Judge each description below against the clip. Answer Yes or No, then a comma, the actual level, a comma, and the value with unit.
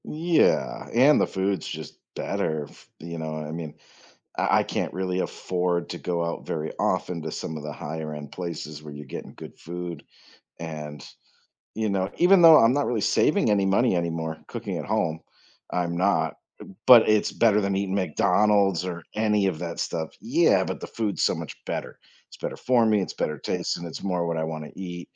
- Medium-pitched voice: No, very low, 90 Hz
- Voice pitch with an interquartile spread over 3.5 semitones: Yes, average, 4.0 semitones